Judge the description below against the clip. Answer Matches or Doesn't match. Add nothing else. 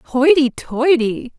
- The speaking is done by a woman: Matches